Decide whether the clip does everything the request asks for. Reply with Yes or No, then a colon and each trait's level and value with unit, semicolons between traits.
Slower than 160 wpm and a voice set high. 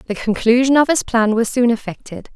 No: fast, 205 wpm; high, 240 Hz